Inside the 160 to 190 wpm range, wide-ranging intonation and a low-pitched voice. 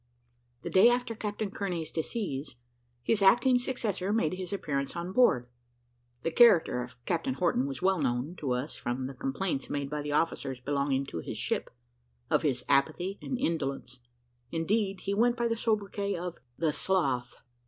No: average, 165 wpm; wide, 6.7 semitones; medium, 170 Hz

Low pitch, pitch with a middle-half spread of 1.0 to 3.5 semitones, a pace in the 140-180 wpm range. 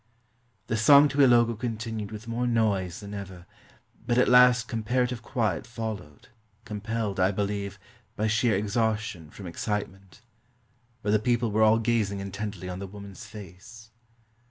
Yes: low, 110 Hz; average, 2.7 semitones; average, 145 wpm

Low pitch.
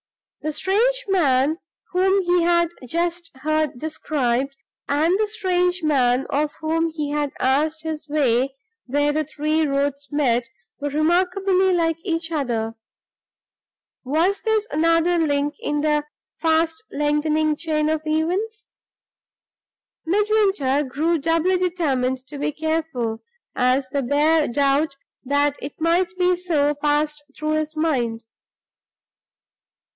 No: very high, 310 Hz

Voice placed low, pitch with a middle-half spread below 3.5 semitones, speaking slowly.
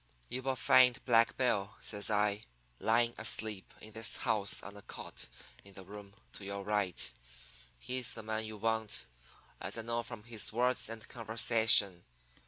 No: low, 110 Hz; narrow, 2.4 semitones; average, 165 wpm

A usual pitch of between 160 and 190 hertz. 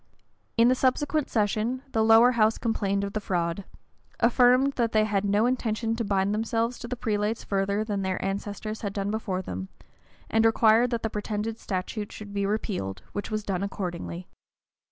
No: high, 215 Hz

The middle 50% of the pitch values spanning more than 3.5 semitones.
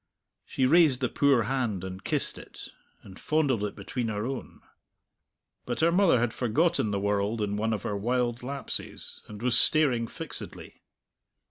Yes: average, 4.5 semitones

